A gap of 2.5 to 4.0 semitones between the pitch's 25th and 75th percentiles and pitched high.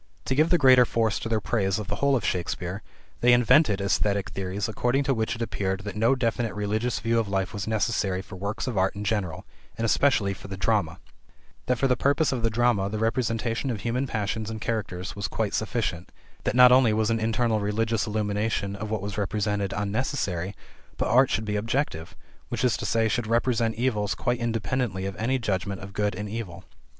No: average, 2.9 semitones; low, 110 Hz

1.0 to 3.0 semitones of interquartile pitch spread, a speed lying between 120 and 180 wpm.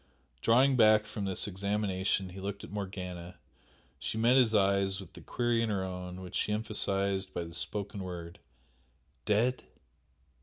Yes: narrow, 2.4 semitones; average, 155 wpm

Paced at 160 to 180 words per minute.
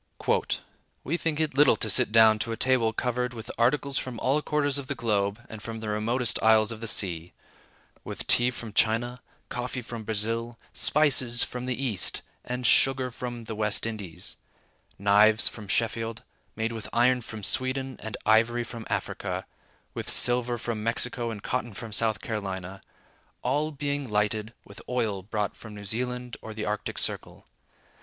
Yes: average, 165 wpm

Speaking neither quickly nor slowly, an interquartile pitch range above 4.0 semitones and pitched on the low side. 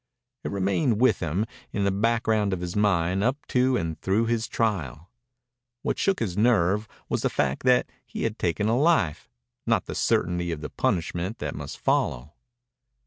Yes: average, 175 wpm; average, 5.0 semitones; low, 100 Hz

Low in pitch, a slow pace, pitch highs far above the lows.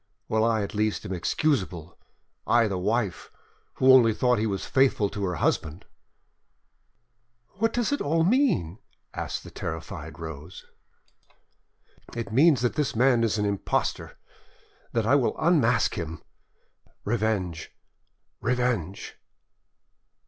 Yes: low, 110 Hz; slow, 125 wpm; wide, 5.7 semitones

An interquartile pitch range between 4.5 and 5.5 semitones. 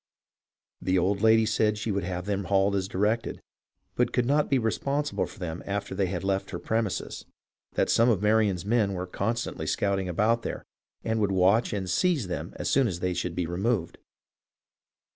No: average, 3.3 semitones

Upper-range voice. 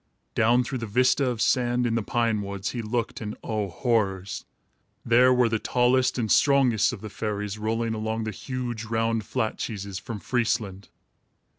No: low, 115 Hz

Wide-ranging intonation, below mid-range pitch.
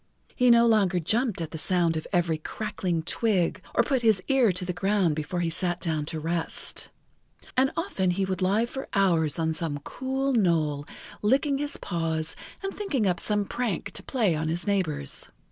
No: wide, 5.9 semitones; medium, 185 Hz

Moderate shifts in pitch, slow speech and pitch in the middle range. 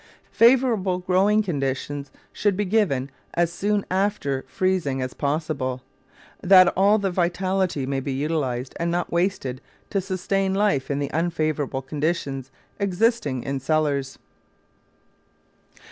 No: wide, 5.8 semitones; slow, 120 wpm; medium, 170 Hz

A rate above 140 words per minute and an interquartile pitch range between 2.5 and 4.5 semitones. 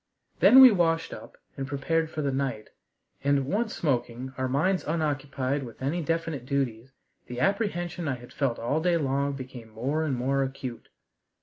Yes: average, 170 wpm; average, 3.9 semitones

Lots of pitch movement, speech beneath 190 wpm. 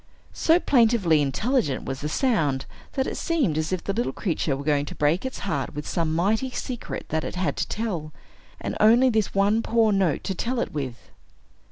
No: wide, 7.4 semitones; average, 200 wpm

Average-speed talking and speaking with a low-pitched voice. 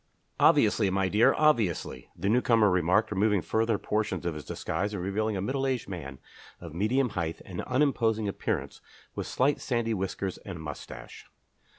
Yes: average, 160 wpm; low, 105 Hz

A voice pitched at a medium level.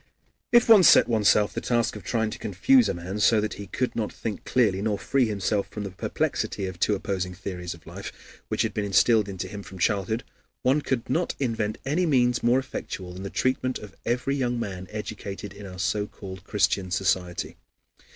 No: low, 105 Hz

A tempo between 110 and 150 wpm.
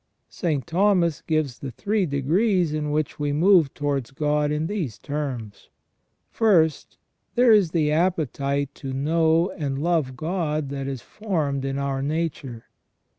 Yes: average, 145 wpm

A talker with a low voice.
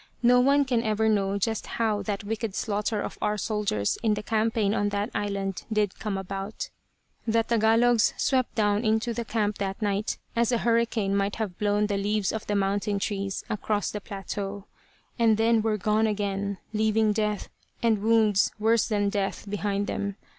No: high, 210 Hz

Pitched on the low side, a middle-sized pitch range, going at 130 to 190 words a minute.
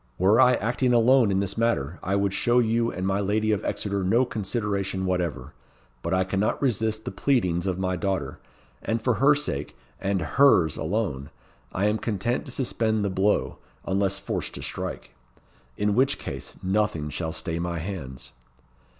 Yes: low, 100 Hz; average, 3.7 semitones; average, 170 wpm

